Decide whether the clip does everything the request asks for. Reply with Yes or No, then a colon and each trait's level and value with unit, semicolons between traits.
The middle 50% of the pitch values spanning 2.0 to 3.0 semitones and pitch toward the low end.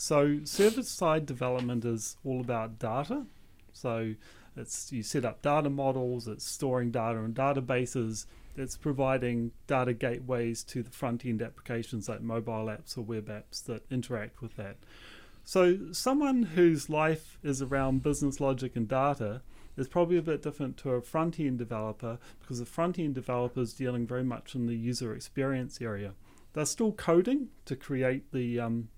No: average, 3.7 semitones; low, 125 Hz